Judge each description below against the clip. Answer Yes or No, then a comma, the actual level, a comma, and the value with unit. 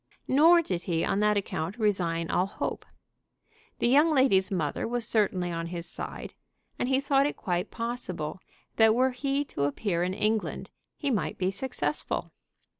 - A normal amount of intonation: No, wide, 6.5 semitones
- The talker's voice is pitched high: Yes, high, 210 Hz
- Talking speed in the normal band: Yes, average, 165 wpm